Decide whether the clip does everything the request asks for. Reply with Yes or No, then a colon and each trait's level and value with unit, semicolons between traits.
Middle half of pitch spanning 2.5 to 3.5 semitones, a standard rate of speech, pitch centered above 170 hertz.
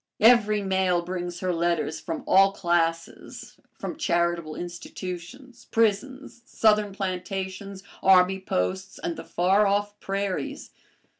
No: average, 2.9 semitones; slow, 115 wpm; high, 190 Hz